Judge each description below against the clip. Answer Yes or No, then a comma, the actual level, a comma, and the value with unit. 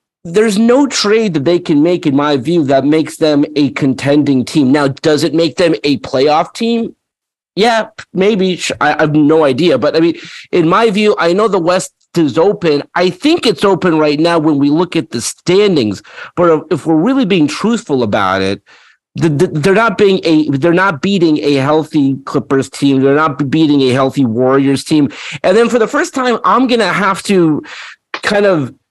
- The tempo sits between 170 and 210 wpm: Yes, average, 190 wpm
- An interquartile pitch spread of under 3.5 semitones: No, wide, 5.4 semitones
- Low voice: No, medium, 165 Hz